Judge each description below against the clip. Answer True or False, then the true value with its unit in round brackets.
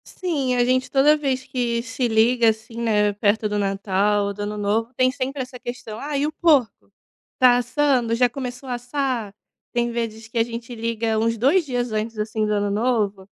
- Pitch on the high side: True (235 Hz)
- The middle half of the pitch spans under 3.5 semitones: True (2.9 semitones)